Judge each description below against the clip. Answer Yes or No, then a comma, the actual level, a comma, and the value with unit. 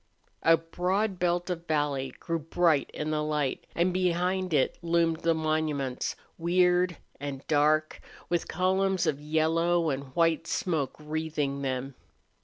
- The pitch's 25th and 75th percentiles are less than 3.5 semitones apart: Yes, average, 2.8 semitones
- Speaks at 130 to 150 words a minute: Yes, slow, 135 wpm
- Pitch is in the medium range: Yes, medium, 160 Hz